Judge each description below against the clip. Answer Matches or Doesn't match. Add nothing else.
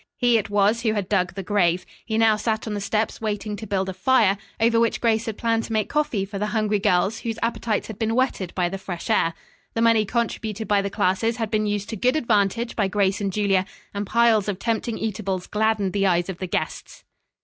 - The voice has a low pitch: Doesn't match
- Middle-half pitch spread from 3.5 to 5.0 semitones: Doesn't match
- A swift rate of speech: Matches